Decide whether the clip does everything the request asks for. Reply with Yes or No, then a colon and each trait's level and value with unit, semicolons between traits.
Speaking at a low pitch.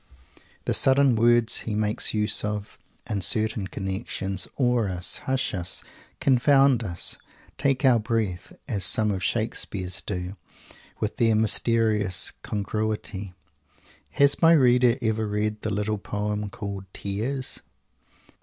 Yes: low, 110 Hz